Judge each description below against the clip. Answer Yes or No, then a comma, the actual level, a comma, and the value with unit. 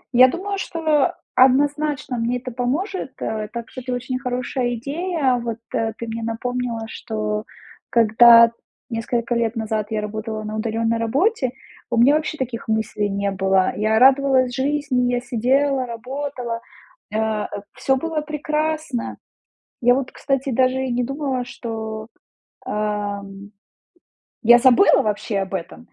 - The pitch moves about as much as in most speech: Yes, average, 3.4 semitones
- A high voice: Yes, high, 245 Hz